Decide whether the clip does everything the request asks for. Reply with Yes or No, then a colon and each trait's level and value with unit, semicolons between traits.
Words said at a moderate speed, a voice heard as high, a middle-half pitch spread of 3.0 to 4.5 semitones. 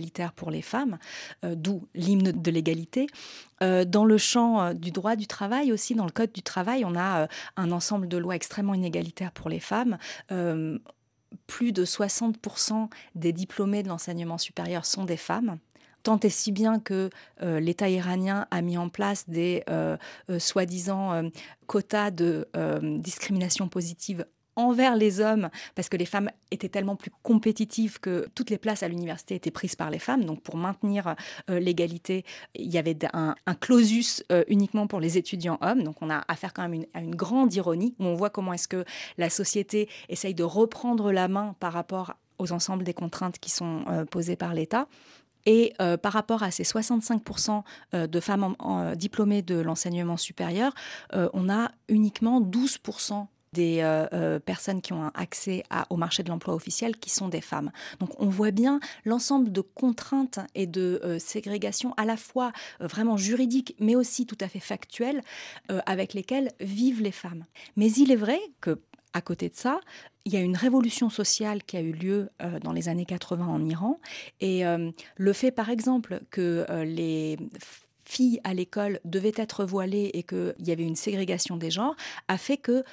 Yes: average, 190 wpm; high, 195 Hz; average, 4.2 semitones